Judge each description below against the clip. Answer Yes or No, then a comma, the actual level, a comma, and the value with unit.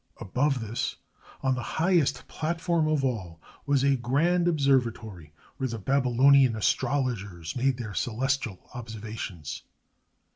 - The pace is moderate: No, slow, 115 wpm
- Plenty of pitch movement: No, average, 4.2 semitones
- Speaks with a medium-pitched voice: No, low, 130 Hz